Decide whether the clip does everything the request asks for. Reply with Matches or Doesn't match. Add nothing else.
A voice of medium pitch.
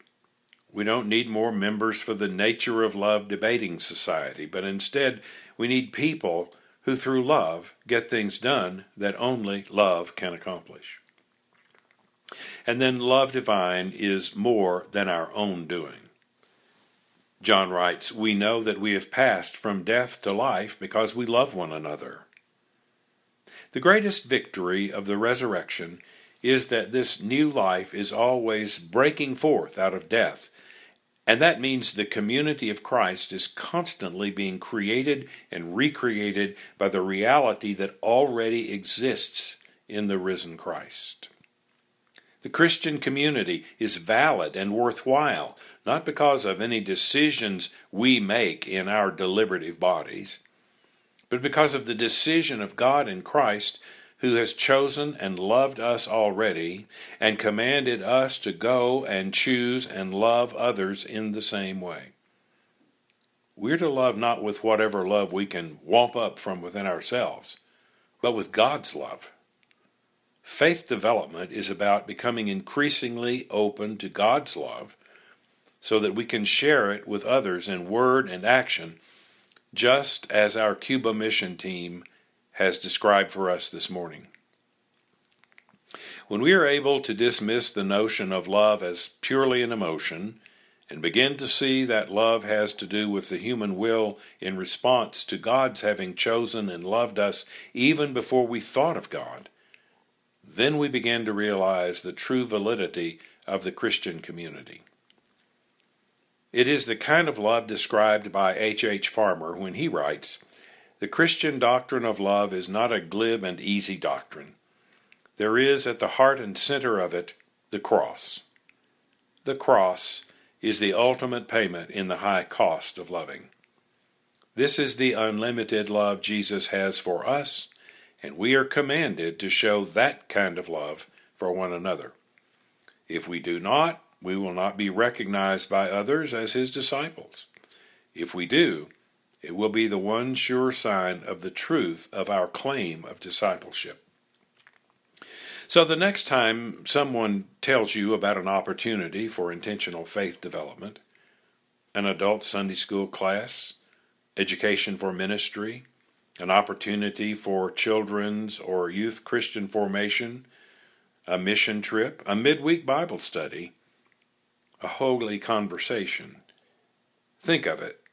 Doesn't match